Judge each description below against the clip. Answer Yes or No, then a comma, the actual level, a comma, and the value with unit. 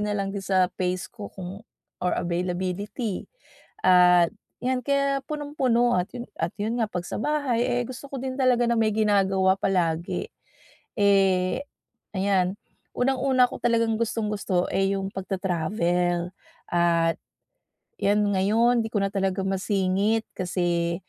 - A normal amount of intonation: Yes, average, 4.2 semitones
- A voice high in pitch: Yes, high, 195 Hz